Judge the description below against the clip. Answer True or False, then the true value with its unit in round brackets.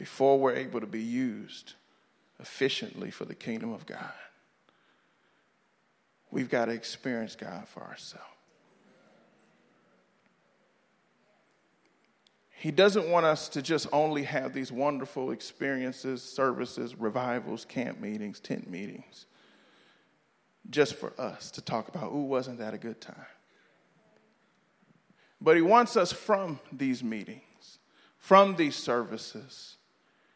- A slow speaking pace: True (115 wpm)